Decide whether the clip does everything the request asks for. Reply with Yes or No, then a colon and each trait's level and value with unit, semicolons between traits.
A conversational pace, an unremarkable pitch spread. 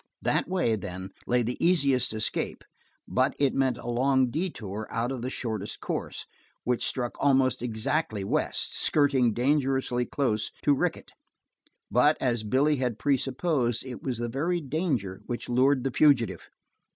Yes: average, 150 wpm; average, 3.0 semitones